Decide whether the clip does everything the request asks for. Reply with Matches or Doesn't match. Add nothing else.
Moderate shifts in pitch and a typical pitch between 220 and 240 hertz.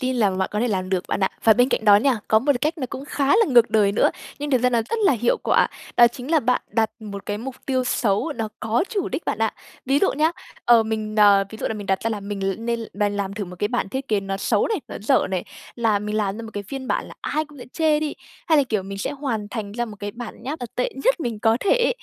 Matches